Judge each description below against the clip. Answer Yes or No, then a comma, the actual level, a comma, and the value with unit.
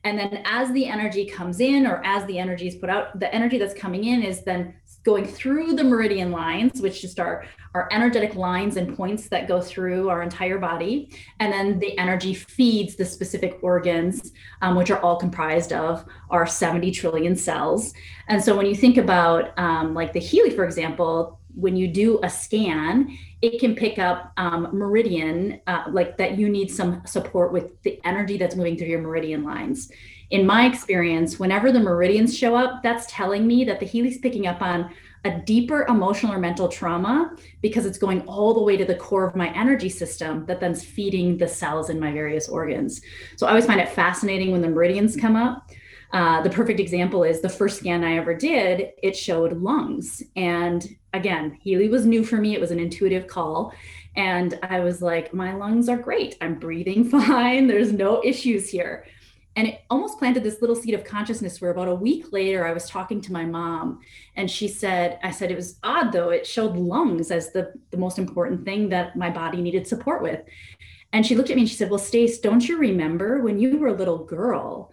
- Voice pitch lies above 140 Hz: Yes, high, 190 Hz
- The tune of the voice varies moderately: Yes, average, 4.4 semitones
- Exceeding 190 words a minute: Yes, fast, 205 wpm